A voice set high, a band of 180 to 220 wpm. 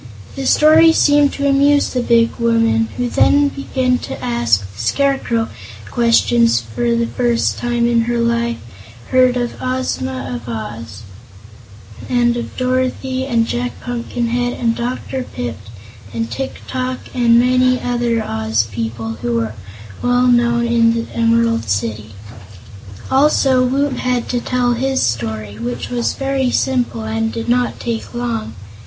No: high, 235 Hz; average, 145 wpm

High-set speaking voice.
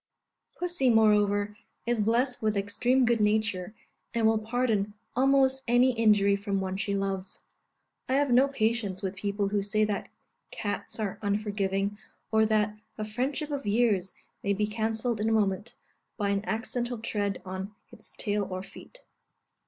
Yes: high, 215 Hz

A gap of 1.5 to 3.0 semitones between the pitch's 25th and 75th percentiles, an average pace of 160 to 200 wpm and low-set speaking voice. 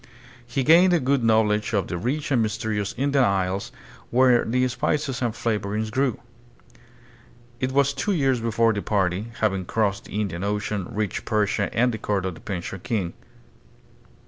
No: average, 4.1 semitones; average, 165 wpm; low, 110 Hz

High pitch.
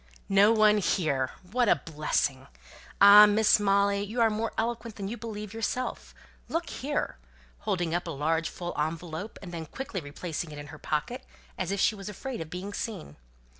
Yes: high, 200 Hz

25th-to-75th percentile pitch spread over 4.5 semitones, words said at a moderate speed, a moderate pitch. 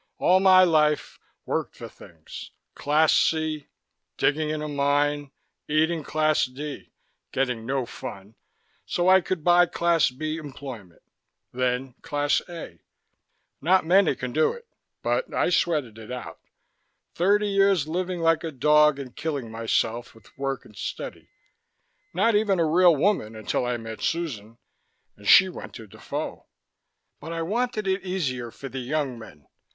Yes: wide, 5.4 semitones; average, 150 wpm; medium, 150 Hz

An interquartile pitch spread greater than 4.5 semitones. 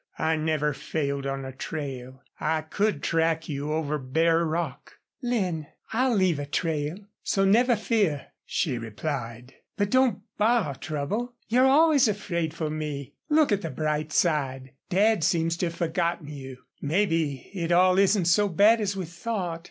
Yes: wide, 5.5 semitones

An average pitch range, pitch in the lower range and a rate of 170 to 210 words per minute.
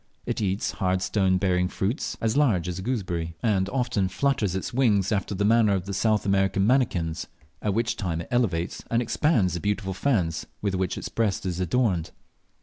Yes: average, 3.6 semitones; low, 100 Hz; average, 190 wpm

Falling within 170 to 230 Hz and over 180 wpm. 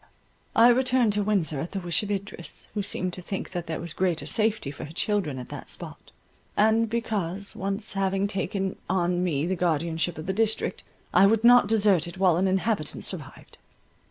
Yes: high, 190 Hz; average, 190 wpm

